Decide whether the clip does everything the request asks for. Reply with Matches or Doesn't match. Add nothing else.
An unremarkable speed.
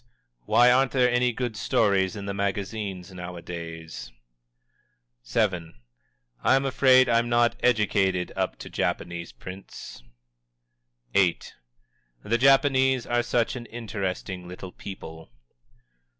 Doesn't match